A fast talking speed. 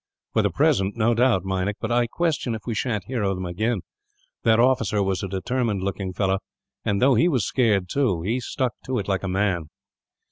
Yes: fast, 210 wpm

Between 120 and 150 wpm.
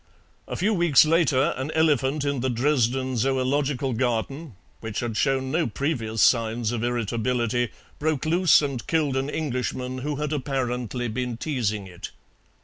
Yes: average, 145 wpm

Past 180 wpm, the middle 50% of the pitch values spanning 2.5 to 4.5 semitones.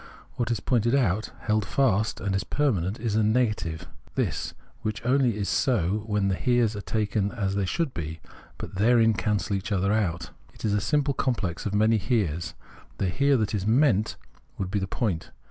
Yes: average, 195 wpm; average, 3.5 semitones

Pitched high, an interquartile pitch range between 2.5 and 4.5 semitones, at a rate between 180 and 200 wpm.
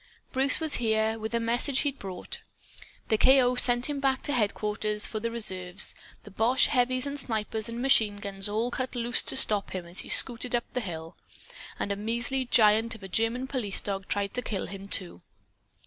Yes: high, 225 Hz; average, 3.5 semitones; average, 195 wpm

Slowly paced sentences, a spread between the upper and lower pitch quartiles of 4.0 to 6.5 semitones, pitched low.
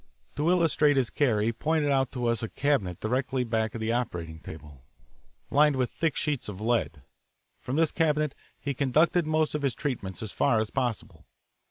No: average, 185 wpm; average, 5.1 semitones; low, 130 Hz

